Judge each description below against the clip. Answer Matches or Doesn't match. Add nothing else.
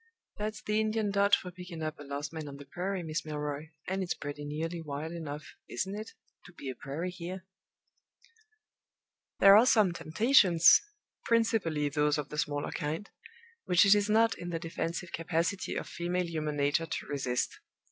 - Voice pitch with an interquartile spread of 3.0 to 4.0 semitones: Doesn't match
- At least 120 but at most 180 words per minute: Matches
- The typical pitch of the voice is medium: Matches